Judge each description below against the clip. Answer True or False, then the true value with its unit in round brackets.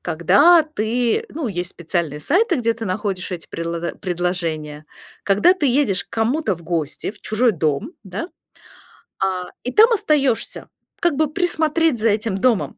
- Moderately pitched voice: False (215 Hz)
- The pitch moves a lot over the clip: True (8.7 semitones)